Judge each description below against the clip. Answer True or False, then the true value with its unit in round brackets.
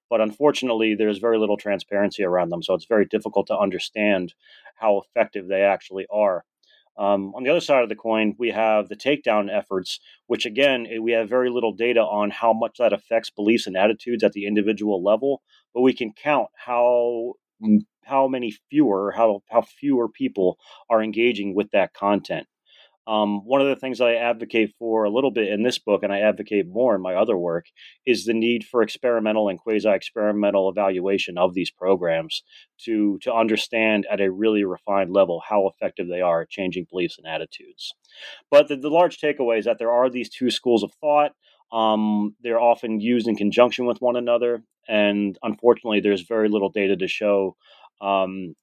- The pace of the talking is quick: False (185 wpm)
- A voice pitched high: False (110 Hz)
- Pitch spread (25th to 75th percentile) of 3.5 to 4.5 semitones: False (3.0 semitones)